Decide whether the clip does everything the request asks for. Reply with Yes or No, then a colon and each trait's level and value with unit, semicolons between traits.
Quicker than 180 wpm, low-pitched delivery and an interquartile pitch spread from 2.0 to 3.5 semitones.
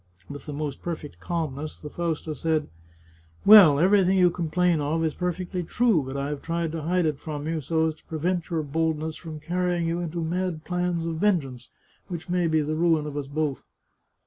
No: fast, 205 wpm; medium, 160 Hz; narrow, 2.6 semitones